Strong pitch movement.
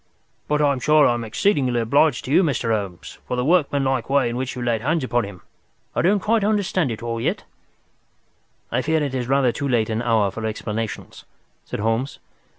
No: average, 4.4 semitones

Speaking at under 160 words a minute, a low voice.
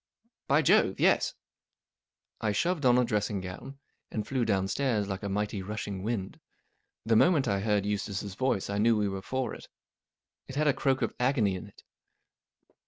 No: average, 180 wpm; low, 105 Hz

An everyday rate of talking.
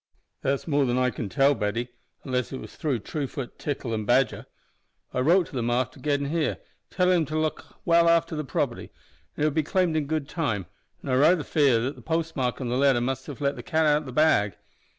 No: fast, 230 wpm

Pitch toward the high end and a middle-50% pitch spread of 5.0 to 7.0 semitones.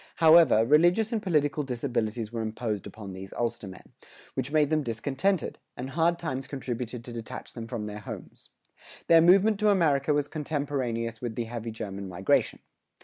No: low, 130 Hz; wide, 5.5 semitones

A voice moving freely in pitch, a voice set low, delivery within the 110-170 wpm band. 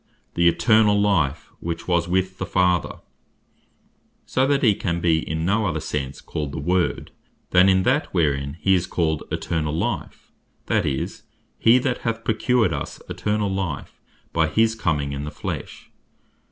No: average, 5.0 semitones; very low, 90 Hz; average, 160 wpm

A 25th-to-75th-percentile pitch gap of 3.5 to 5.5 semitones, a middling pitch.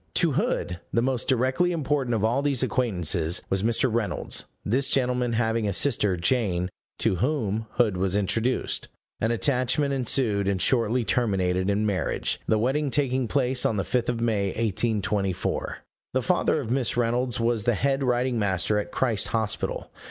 No: average, 4.1 semitones; low, 115 Hz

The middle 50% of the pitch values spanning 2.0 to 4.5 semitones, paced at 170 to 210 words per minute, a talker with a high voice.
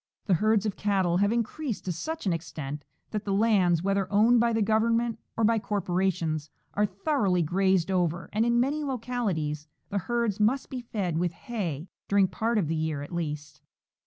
No: average, 4.9 semitones; average, 185 wpm; high, 200 Hz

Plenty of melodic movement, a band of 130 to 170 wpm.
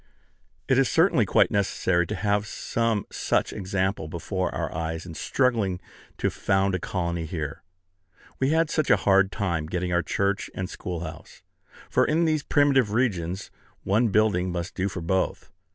No: average, 4.2 semitones; average, 160 wpm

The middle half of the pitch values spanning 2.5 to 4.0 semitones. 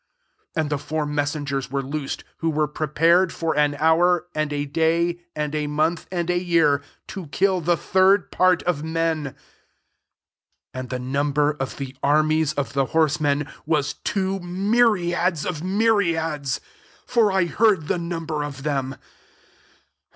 Yes: average, 3.2 semitones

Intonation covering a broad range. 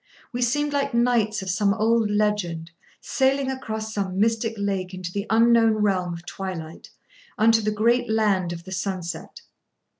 No: average, 3.5 semitones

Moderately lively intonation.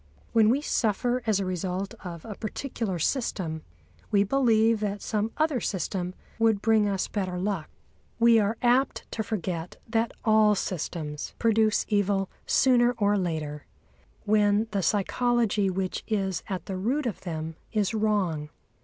Yes: average, 3.4 semitones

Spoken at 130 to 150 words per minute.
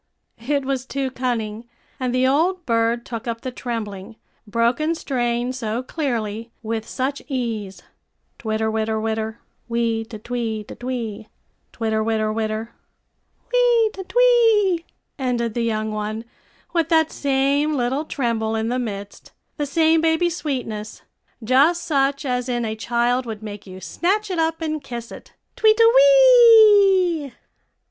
Yes: average, 145 wpm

